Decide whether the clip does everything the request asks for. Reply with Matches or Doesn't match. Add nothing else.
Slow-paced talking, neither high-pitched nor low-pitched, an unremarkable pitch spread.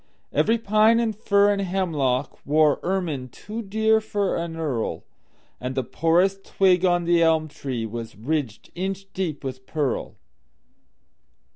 Doesn't match